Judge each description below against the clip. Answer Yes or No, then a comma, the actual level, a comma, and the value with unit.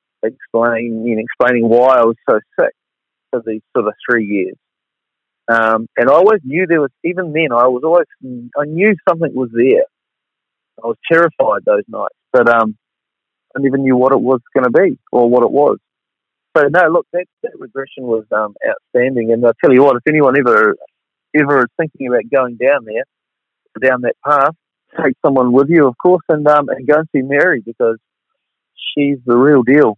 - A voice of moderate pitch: No, low, 130 Hz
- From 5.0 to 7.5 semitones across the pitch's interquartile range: Yes, average, 5.3 semitones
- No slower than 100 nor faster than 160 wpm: No, average, 195 wpm